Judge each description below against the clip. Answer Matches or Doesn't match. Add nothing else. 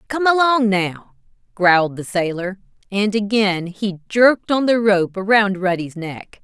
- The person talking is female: Matches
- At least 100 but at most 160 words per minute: Matches